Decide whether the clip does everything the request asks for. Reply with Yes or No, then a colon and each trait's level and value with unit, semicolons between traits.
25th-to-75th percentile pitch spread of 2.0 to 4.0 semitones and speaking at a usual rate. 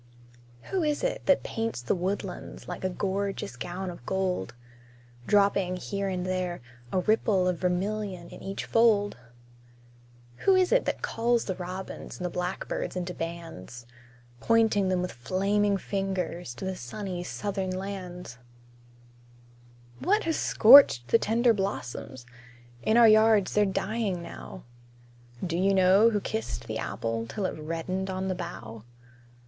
Yes: average, 2.8 semitones; average, 145 wpm